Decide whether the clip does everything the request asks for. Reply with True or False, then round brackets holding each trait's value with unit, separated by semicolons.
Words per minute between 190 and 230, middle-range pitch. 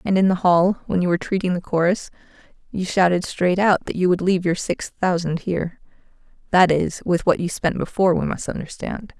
True (200 wpm; 180 Hz)